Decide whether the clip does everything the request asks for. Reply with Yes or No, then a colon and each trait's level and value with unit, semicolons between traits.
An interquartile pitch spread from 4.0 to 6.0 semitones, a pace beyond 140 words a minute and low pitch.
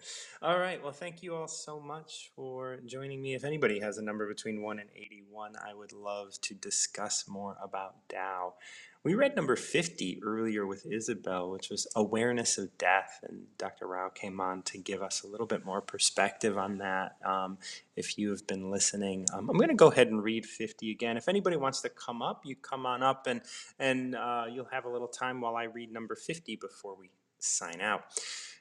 Yes: average, 4.7 semitones; fast, 205 wpm; low, 110 Hz